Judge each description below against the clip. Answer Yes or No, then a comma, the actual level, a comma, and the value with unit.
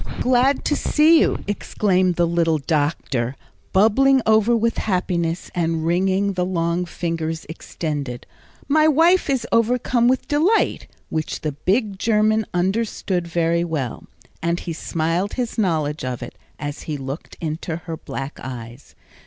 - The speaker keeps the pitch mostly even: No, wide, 5.6 semitones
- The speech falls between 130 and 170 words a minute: Yes, average, 140 wpm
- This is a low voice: No, medium, 175 Hz